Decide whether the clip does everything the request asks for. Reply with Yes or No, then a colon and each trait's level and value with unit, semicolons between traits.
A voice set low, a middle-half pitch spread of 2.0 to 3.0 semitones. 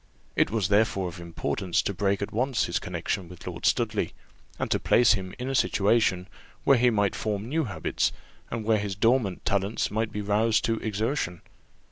Yes: low, 105 Hz; average, 2.7 semitones